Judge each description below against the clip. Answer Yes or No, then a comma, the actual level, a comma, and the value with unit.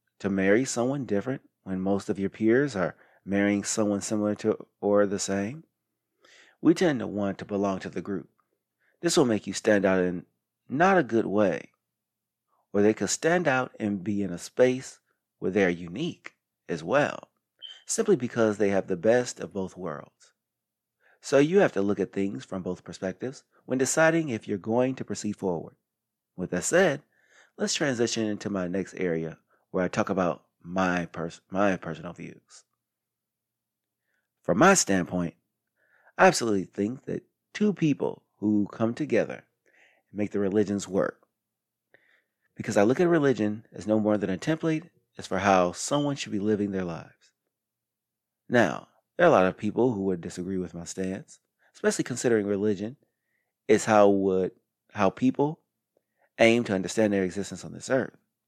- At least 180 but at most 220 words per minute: No, average, 170 wpm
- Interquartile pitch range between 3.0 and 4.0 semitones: Yes, average, 3.5 semitones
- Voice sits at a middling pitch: No, low, 105 Hz